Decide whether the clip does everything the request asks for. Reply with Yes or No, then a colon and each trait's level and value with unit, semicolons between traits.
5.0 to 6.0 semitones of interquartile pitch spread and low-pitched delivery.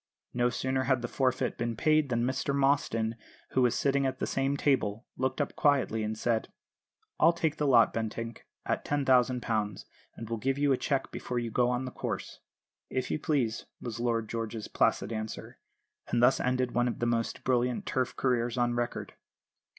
No: narrow, 2.5 semitones; low, 125 Hz